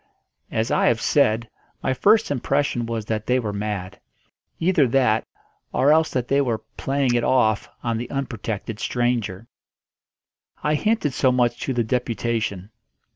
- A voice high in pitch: No, low, 120 Hz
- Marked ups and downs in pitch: No, average, 3.5 semitones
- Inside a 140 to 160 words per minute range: Yes, average, 150 wpm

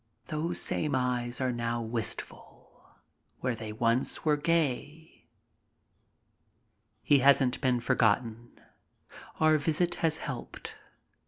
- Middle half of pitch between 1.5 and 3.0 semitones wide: No, average, 4.4 semitones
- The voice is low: Yes, low, 130 Hz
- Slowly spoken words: Yes, slow, 100 wpm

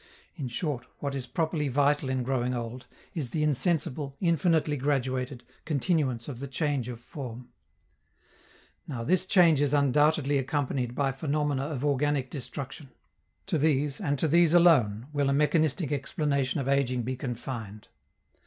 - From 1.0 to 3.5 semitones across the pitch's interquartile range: Yes, average, 2.9 semitones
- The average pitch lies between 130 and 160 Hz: Yes, medium, 140 Hz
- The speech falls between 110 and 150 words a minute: Yes, average, 145 wpm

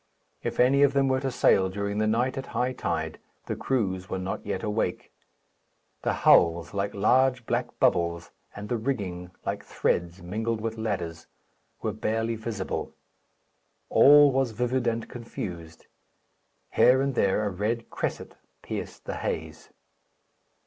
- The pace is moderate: Yes, average, 145 wpm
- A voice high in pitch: No, low, 110 Hz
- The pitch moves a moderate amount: Yes, average, 5.0 semitones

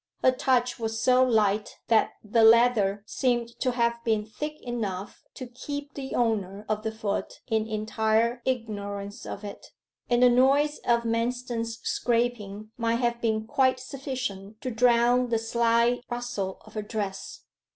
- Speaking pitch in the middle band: No, high, 235 Hz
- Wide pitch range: No, narrow, 2.4 semitones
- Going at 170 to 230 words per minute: No, average, 150 wpm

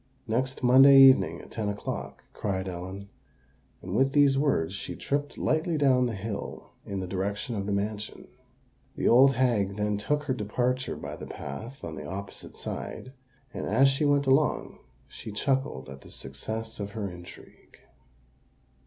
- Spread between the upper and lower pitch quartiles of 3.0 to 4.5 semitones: No, average, 5.1 semitones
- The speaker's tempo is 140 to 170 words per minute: Yes, average, 160 wpm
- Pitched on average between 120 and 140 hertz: No, low, 110 Hz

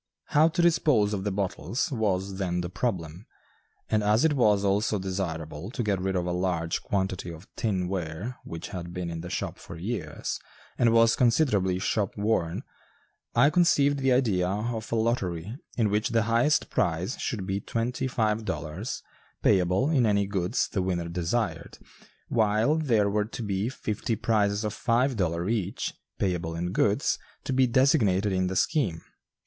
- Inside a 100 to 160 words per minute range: No, average, 170 wpm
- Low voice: Yes, low, 105 Hz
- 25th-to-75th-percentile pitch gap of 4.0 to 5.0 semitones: Yes, average, 4.3 semitones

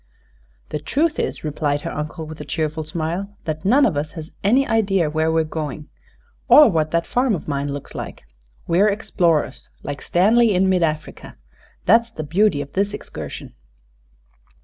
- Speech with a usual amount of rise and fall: Yes, average, 4.9 semitones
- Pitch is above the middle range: No, medium, 165 Hz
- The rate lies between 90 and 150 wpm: No, average, 170 wpm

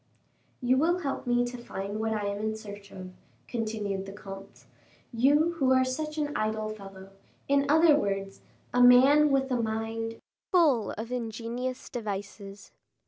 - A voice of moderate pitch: No, high, 230 Hz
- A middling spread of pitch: Yes, average, 4.4 semitones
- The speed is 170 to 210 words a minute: No, average, 155 wpm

